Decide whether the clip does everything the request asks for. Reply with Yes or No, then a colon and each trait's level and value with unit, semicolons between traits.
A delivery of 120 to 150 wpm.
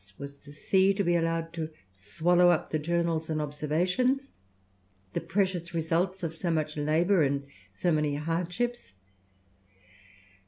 Yes: slow, 135 wpm